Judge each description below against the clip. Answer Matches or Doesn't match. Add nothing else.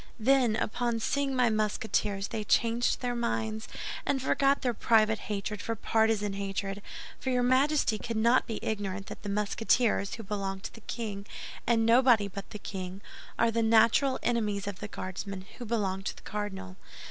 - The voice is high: Matches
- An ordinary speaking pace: Matches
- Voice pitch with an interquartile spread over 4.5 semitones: Doesn't match